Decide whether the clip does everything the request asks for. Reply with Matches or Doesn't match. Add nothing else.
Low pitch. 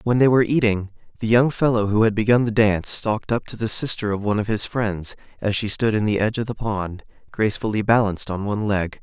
Matches